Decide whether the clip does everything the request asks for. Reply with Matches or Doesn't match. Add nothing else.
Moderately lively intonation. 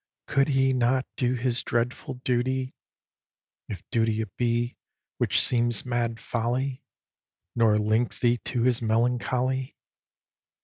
Doesn't match